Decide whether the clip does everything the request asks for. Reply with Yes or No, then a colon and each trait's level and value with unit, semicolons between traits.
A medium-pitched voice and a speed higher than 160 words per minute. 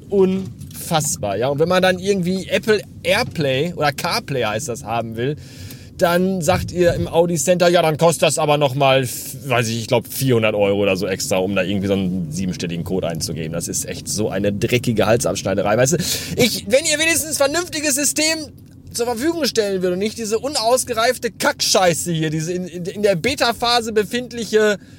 Yes: medium, 170 Hz; average, 180 wpm